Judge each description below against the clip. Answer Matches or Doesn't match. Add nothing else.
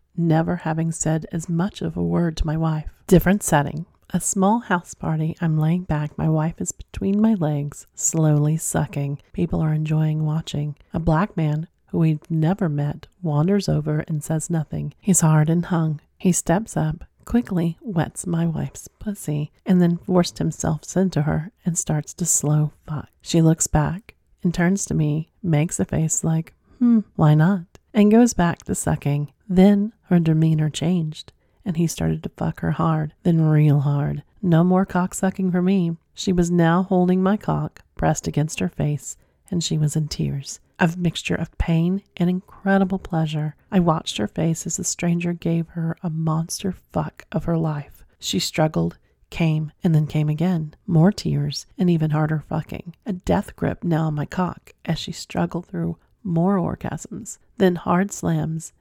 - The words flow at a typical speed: Matches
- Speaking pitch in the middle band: Matches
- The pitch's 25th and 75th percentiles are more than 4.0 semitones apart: Doesn't match